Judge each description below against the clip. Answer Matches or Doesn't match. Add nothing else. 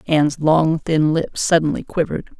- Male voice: Doesn't match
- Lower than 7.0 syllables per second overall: Matches